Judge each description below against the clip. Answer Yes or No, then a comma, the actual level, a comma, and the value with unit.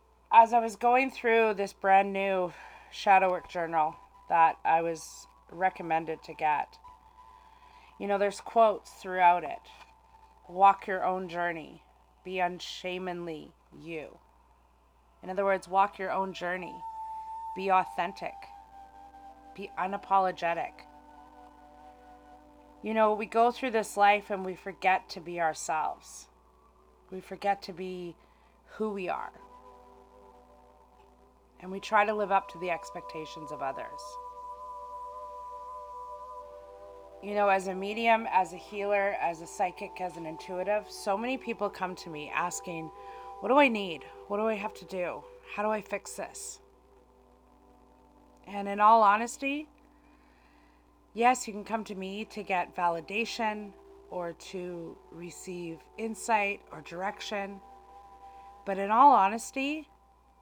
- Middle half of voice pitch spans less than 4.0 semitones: No, average, 4.5 semitones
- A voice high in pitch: Yes, high, 195 Hz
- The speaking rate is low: Yes, slow, 130 wpm